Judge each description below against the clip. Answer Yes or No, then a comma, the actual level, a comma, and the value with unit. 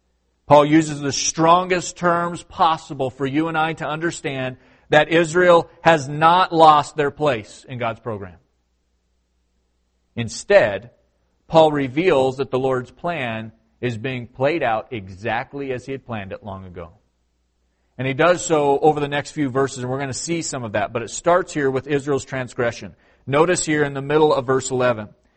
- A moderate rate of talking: Yes, average, 175 wpm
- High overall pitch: No, low, 135 Hz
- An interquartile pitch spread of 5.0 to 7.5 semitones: Yes, wide, 5.6 semitones